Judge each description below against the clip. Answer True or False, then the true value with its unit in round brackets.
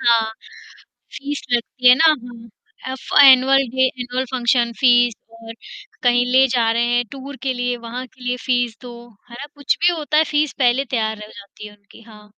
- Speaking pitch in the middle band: False (245 Hz)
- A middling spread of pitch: False (2.0 semitones)